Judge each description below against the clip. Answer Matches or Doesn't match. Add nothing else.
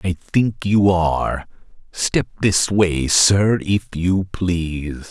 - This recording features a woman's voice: Doesn't match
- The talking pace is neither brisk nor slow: Doesn't match